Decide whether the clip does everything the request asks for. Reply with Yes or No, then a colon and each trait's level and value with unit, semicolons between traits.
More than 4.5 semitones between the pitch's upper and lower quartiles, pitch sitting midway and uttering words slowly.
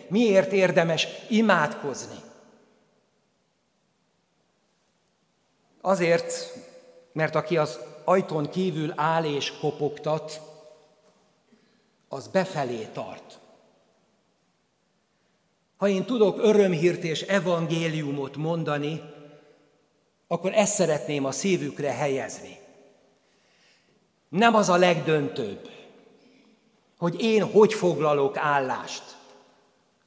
Yes: wide, 5.4 semitones; medium, 175 Hz; slow, 75 wpm